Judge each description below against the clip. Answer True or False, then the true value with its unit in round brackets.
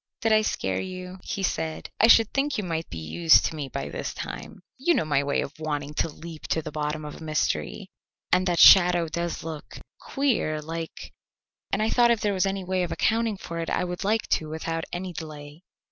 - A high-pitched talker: False (170 Hz)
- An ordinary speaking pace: False (220 wpm)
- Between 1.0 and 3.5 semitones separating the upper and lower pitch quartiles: False (3.9 semitones)